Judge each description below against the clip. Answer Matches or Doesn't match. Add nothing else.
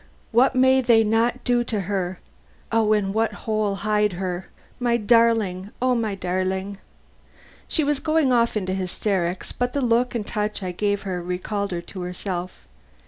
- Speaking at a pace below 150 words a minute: Doesn't match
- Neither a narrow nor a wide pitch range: Matches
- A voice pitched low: Doesn't match